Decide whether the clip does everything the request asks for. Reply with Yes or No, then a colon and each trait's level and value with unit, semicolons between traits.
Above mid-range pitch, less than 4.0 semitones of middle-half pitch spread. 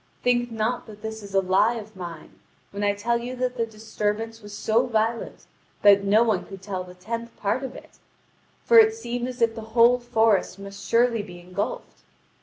Yes: high, 220 Hz; average, 2.8 semitones